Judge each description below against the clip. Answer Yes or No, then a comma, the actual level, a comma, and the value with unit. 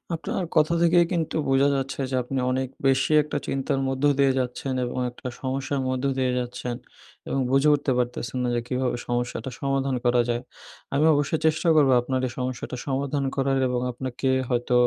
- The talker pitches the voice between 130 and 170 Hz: Yes, low, 135 Hz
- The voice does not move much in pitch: Yes, narrow, 1.9 semitones